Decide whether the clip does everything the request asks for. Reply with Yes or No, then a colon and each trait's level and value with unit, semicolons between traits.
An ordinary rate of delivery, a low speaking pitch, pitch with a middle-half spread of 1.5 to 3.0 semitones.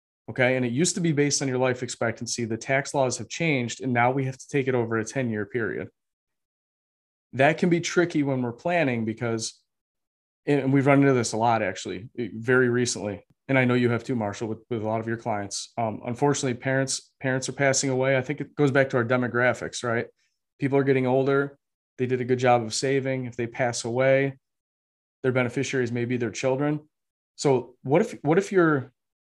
No: fast, 210 wpm; low, 130 Hz; average, 2.7 semitones